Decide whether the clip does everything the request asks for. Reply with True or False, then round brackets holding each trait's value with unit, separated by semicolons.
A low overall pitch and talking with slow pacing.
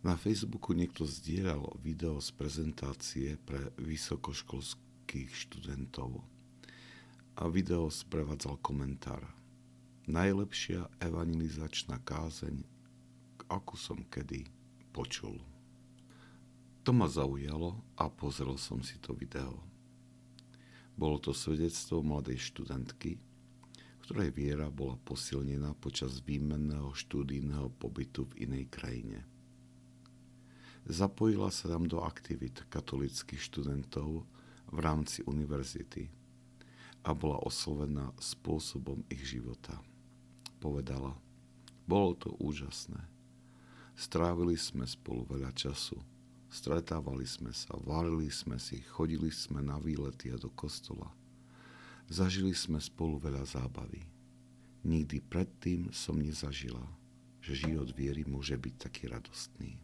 True (75 Hz; 100 wpm)